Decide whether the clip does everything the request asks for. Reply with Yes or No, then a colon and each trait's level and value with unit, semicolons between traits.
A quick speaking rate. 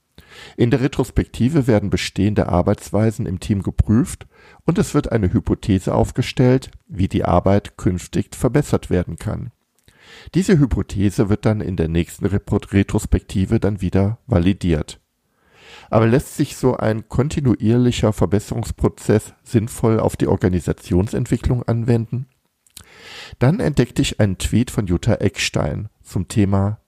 No: slow, 125 wpm